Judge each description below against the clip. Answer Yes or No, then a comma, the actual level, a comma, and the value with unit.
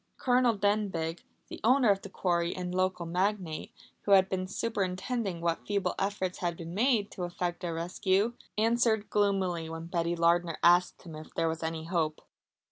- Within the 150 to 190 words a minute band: Yes, average, 170 wpm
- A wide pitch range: No, average, 3.1 semitones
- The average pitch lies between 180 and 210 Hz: Yes, medium, 185 Hz